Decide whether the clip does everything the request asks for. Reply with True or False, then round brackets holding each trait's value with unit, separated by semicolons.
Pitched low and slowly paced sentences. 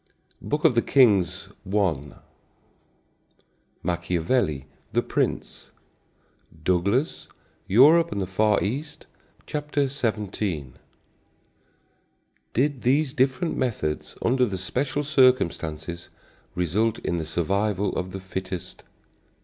True (100 Hz; 90 wpm)